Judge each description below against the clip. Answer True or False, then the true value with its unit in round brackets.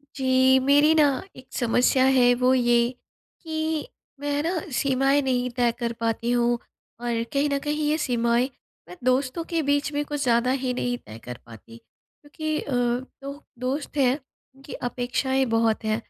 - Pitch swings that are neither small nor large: True (3.0 semitones)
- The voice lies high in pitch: True (260 Hz)